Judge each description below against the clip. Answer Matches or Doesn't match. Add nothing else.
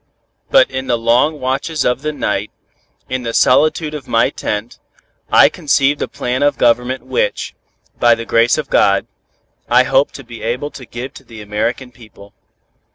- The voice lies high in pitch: Doesn't match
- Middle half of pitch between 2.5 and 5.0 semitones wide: Matches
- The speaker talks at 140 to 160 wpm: Doesn't match